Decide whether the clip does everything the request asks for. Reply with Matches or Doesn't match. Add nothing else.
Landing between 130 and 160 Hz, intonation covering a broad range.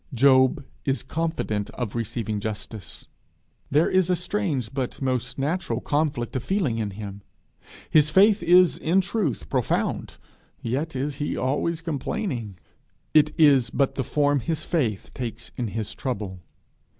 Matches